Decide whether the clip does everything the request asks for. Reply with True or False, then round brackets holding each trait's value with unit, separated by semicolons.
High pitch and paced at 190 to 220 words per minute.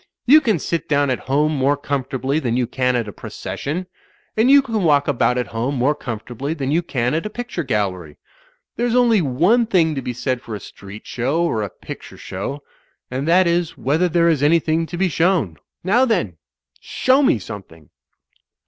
False (145 Hz; 200 wpm)